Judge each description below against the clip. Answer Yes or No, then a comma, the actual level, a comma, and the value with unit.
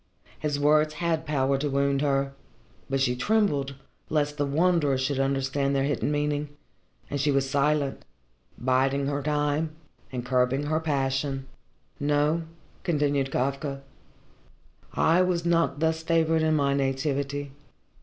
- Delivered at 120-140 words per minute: Yes, slow, 135 wpm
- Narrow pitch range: Yes, narrow, 2.0 semitones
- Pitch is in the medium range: Yes, medium, 145 Hz